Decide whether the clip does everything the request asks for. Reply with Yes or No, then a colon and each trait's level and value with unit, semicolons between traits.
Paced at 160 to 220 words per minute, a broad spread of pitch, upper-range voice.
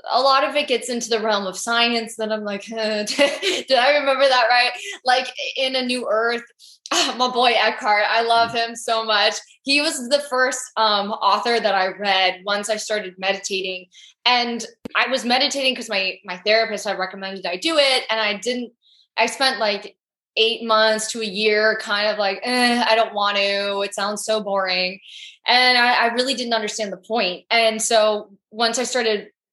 No: average, 190 wpm; average, 3.1 semitones; high, 225 Hz